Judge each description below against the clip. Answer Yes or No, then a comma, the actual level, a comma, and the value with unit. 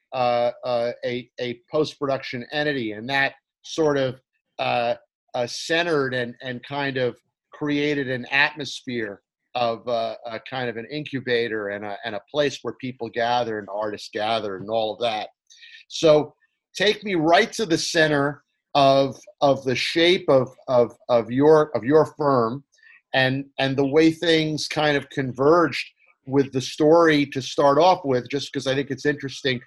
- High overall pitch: No, low, 135 Hz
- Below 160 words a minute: No, average, 165 wpm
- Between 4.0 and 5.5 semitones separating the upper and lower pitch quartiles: No, average, 3.6 semitones